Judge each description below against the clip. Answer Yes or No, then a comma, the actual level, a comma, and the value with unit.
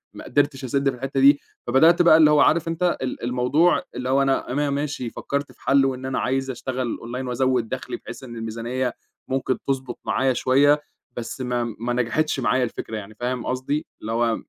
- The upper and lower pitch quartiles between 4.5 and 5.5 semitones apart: No, narrow, 2.4 semitones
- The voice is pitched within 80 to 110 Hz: No, low, 130 Hz